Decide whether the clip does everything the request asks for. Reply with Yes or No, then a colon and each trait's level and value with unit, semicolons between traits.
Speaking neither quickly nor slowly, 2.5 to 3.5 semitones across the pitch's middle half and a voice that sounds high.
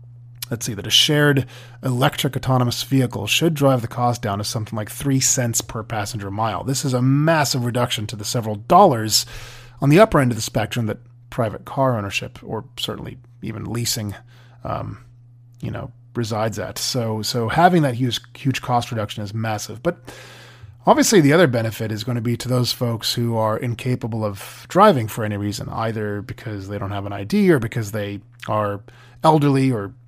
No: average, 185 wpm; average, 2.9 semitones; low, 120 Hz